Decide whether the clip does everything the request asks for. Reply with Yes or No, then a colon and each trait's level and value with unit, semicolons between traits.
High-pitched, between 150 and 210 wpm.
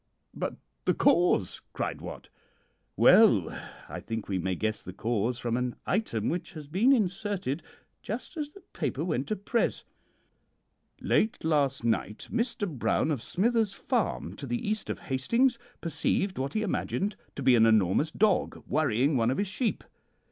No: medium, 160 Hz; average, 160 wpm